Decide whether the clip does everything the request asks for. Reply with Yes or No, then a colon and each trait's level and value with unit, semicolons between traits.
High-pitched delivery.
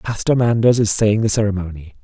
No: low, 105 Hz